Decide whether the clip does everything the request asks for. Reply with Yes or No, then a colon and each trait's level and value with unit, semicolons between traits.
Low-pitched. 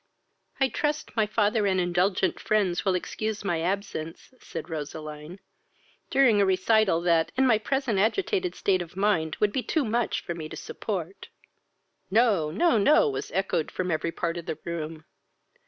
No: high, 190 Hz